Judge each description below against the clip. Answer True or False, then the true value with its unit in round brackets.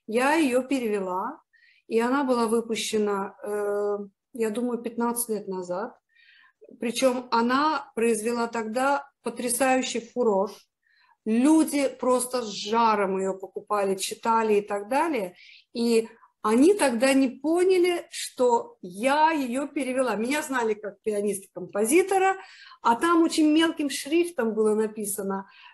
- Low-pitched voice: False (235 Hz)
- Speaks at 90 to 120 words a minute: True (115 wpm)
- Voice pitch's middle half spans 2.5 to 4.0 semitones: False (4.8 semitones)